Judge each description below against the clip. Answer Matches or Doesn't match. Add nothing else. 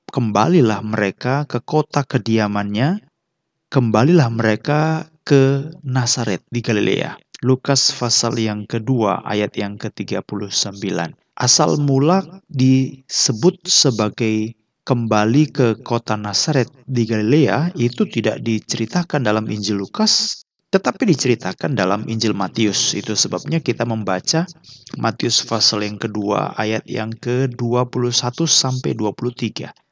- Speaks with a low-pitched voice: Matches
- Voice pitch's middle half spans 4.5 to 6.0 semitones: Matches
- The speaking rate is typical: Matches